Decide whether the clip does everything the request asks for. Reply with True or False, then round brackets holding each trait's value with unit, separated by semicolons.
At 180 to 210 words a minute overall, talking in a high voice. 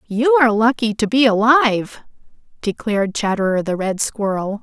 False (145 wpm; 220 Hz)